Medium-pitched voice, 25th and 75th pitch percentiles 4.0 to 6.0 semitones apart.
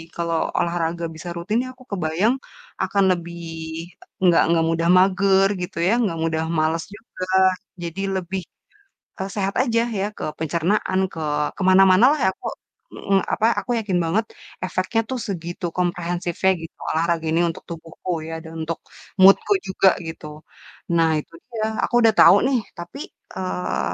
No: medium, 180 Hz; average, 2.8 semitones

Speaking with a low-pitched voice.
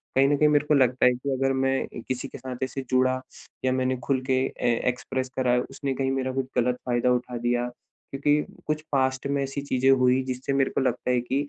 Yes: low, 130 Hz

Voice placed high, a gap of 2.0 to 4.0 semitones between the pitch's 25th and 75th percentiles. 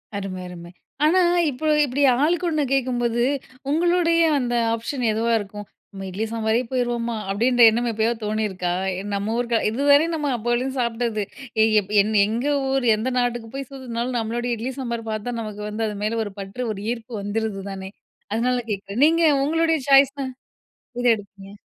Yes: high, 235 Hz; average, 3.4 semitones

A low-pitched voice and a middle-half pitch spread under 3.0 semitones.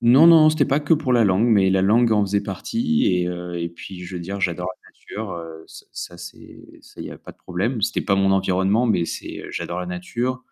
No: very low, 95 Hz; average, 5.1 semitones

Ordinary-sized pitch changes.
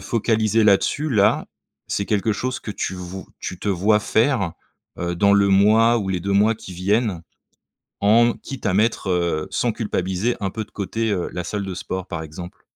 Yes: average, 3.2 semitones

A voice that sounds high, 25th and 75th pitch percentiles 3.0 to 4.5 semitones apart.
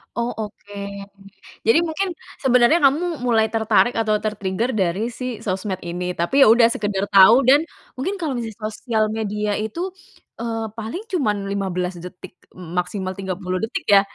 Yes: high, 215 Hz; average, 4.1 semitones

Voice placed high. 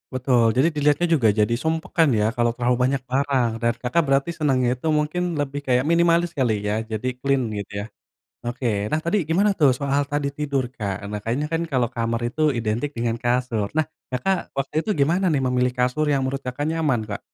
No: low, 130 Hz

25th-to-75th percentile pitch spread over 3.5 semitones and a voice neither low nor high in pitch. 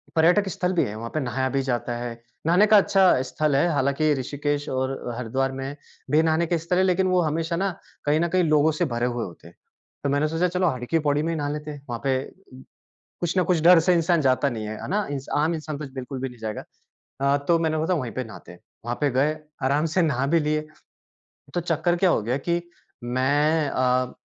Yes: average, 4.3 semitones; medium, 150 Hz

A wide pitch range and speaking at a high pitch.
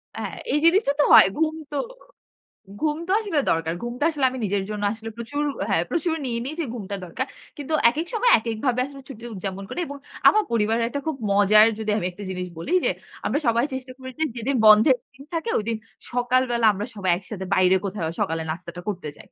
Yes: wide, 6.1 semitones; high, 230 Hz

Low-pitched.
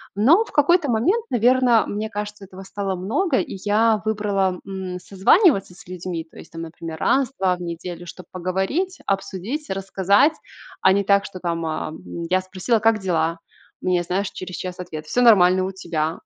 No: high, 190 Hz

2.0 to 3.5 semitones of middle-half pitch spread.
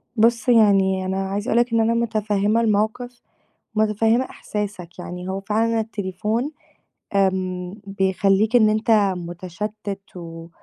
Yes: average, 2.9 semitones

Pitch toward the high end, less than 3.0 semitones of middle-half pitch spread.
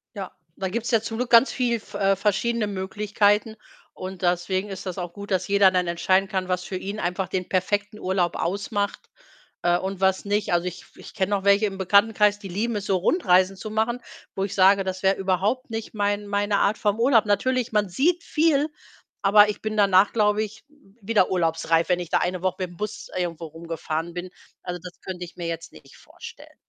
Yes: high, 195 Hz; narrow, 2.5 semitones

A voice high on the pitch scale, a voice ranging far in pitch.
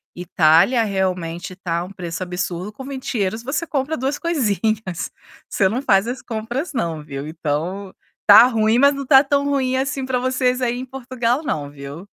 Yes: high, 220 Hz; wide, 6.5 semitones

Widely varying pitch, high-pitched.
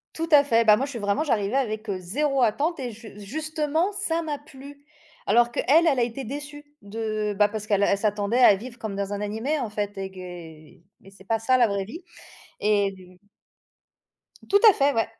Yes: wide, 5.7 semitones; high, 225 Hz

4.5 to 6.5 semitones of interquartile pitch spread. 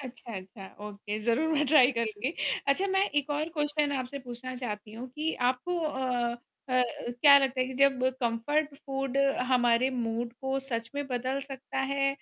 No: average, 2.9 semitones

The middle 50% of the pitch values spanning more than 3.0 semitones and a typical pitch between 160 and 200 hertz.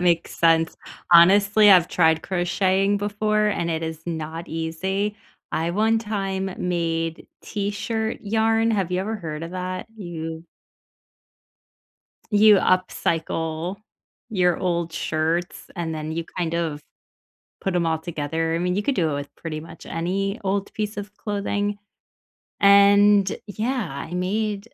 Yes: average, 3.7 semitones; medium, 185 Hz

